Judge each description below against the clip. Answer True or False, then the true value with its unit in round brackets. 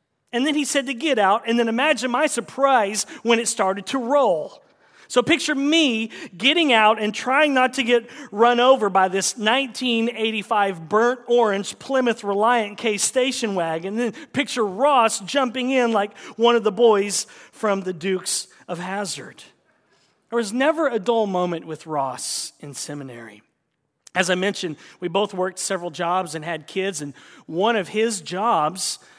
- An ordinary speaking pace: True (165 wpm)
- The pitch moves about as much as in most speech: True (4.8 semitones)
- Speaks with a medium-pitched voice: False (220 Hz)